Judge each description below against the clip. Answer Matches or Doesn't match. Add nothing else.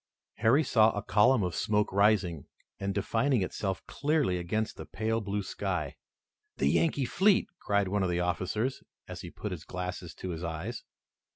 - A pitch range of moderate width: Matches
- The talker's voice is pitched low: Matches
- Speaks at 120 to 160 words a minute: Doesn't match